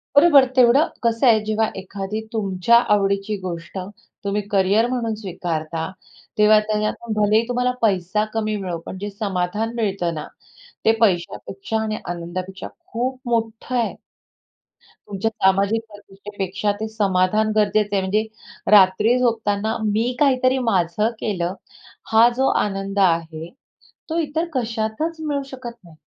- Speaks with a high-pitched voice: Yes, high, 210 Hz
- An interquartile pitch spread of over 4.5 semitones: No, average, 3.0 semitones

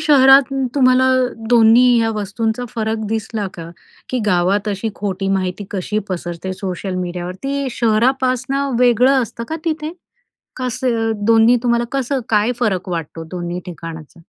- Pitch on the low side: No, high, 225 Hz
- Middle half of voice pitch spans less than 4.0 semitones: No, average, 5.2 semitones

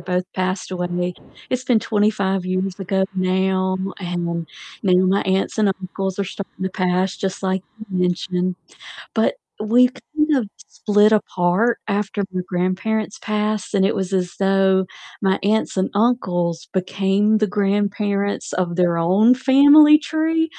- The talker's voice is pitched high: Yes, high, 195 Hz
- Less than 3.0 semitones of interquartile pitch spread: Yes, narrow, 2.5 semitones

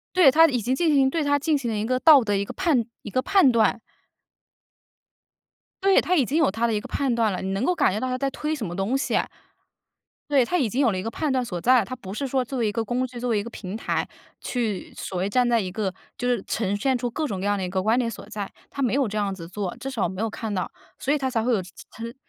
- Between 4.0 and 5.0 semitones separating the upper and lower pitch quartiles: Yes, average, 4.5 semitones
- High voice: Yes, high, 235 Hz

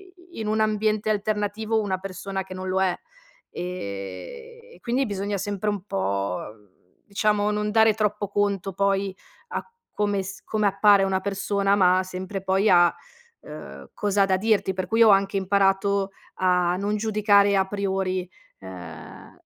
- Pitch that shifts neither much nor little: No, narrow, 2.0 semitones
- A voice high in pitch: Yes, high, 200 Hz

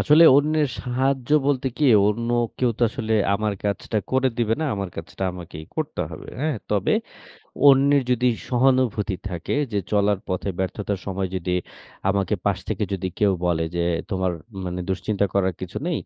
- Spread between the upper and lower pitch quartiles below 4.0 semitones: No, wide, 5.4 semitones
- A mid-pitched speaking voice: No, low, 105 Hz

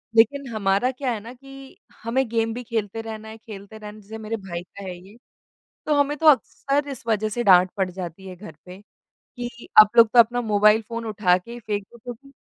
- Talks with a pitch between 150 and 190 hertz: No, high, 220 Hz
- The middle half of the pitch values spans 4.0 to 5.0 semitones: No, average, 3.1 semitones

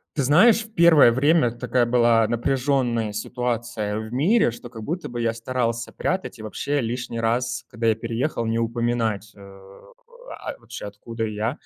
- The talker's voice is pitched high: No, low, 120 Hz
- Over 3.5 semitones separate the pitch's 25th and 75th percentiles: No, average, 3.0 semitones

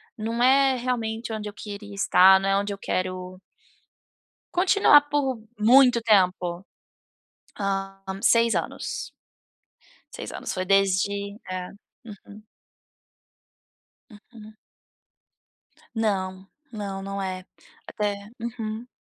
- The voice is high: Yes, high, 205 Hz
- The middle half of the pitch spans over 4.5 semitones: No, average, 3.1 semitones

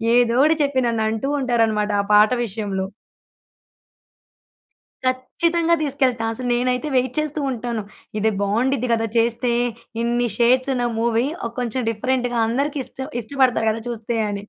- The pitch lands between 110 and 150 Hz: No, high, 240 Hz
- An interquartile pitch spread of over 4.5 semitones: No, narrow, 2.5 semitones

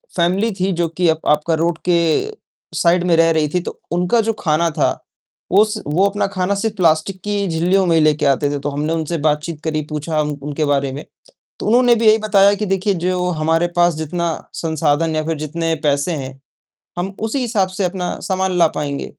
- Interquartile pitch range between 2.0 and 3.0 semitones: No, average, 3.8 semitones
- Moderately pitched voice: Yes, medium, 170 Hz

